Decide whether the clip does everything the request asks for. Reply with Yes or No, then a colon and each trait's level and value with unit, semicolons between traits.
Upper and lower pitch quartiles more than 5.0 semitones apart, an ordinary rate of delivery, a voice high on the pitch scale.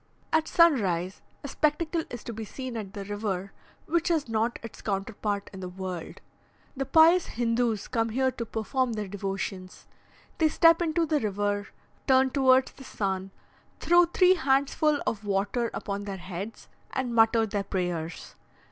Yes: wide, 5.5 semitones; average, 155 wpm; high, 225 Hz